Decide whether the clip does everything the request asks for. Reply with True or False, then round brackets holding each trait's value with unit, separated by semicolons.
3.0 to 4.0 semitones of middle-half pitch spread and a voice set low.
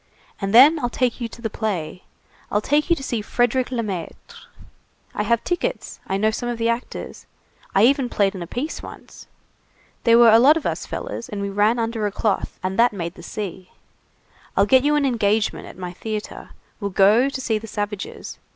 False (3.5 semitones; 225 Hz)